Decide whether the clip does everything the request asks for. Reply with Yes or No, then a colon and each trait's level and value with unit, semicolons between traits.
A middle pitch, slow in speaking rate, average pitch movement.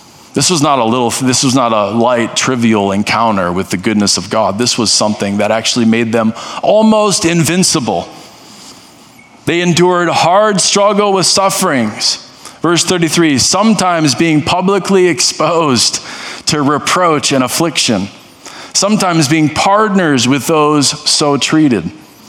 No: medium, 160 Hz; slow, 130 wpm; wide, 7.1 semitones